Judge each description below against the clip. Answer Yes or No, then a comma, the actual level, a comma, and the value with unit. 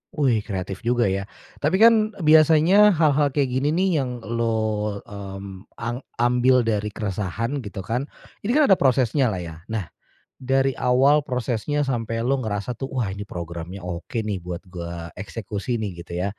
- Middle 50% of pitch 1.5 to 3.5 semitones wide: No, wide, 5.5 semitones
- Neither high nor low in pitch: No, low, 115 Hz